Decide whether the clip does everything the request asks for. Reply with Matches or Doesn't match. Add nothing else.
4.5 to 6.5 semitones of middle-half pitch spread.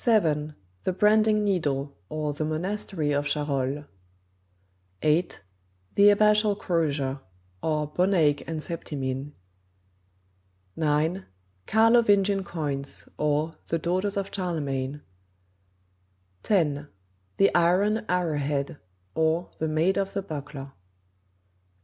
Matches